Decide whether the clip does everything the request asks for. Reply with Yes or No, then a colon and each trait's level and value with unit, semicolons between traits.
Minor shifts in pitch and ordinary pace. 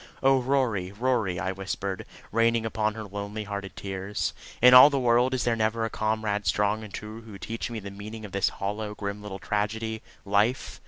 Yes: narrow, 2.2 semitones; average, 195 wpm